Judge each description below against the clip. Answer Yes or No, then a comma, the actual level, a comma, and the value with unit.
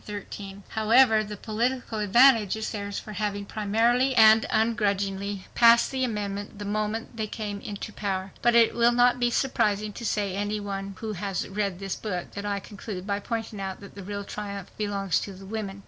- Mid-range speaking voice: No, high, 210 Hz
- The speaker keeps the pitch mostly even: Yes, narrow, 2.0 semitones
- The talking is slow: No, average, 180 wpm